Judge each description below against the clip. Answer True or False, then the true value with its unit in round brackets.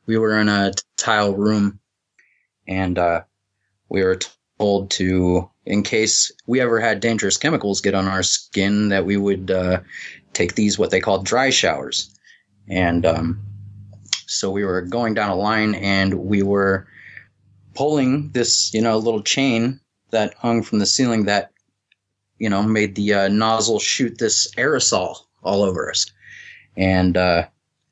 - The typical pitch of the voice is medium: False (100 Hz)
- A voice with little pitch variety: True (2.2 semitones)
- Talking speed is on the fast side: False (155 wpm)